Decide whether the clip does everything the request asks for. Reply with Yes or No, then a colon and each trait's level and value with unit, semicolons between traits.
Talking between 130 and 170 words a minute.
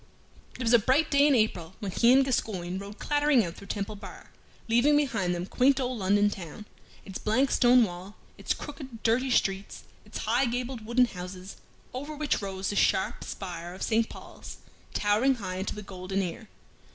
No: average, 185 wpm